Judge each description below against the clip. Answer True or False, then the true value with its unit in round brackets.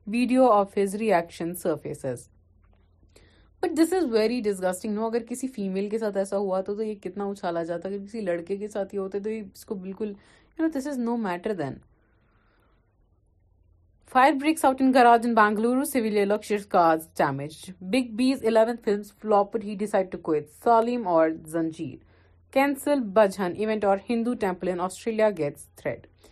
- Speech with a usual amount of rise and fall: False (6.0 semitones)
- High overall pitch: True (200 Hz)